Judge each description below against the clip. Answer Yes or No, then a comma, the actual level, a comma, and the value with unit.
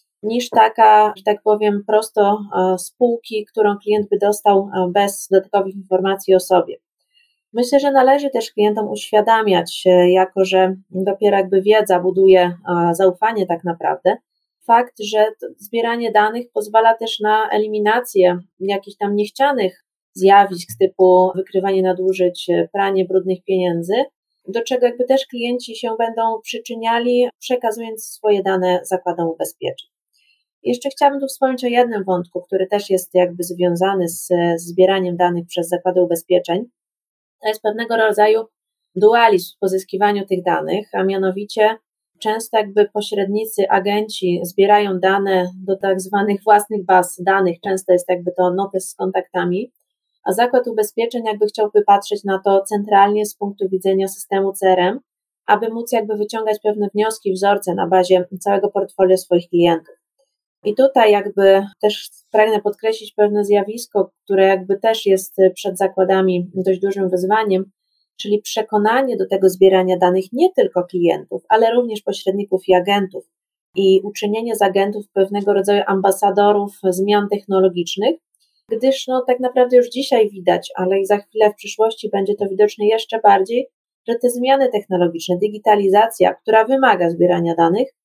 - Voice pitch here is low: No, high, 200 Hz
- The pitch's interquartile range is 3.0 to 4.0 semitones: No, narrow, 2.6 semitones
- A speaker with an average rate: Yes, average, 140 wpm